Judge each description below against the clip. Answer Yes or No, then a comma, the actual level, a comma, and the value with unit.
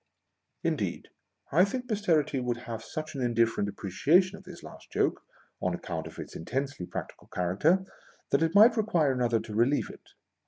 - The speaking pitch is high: No, medium, 140 Hz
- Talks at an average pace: Yes, average, 165 wpm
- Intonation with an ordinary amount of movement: No, wide, 8.0 semitones